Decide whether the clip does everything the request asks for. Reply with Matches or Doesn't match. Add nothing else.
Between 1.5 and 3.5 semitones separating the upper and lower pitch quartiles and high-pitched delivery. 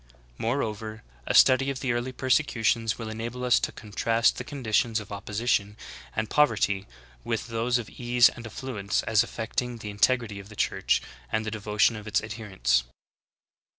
Doesn't match